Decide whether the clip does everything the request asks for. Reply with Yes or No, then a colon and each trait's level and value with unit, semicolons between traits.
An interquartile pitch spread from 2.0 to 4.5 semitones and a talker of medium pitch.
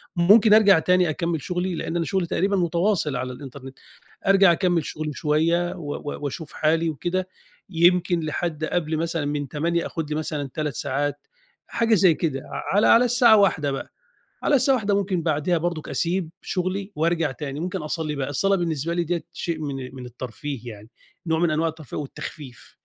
Yes: average, 3.5 semitones; medium, 165 Hz